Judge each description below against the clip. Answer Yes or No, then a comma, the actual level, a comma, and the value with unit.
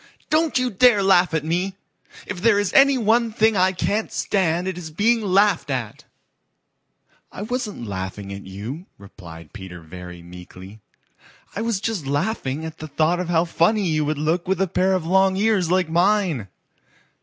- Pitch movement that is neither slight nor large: No, wide, 6.8 semitones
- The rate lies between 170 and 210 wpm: Yes, average, 175 wpm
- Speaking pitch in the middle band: Yes, medium, 180 Hz